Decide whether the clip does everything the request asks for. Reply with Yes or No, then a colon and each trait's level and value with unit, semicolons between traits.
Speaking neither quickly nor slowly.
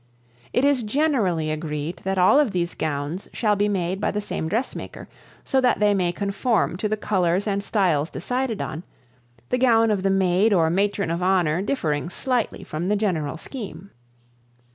Yes: average, 175 wpm